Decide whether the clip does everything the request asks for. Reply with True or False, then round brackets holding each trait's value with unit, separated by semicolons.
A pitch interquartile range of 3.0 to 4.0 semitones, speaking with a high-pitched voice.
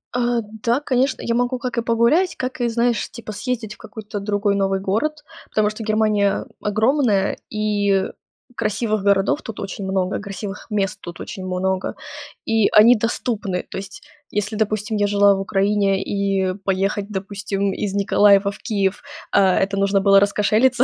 False (2.6 semitones; 205 Hz)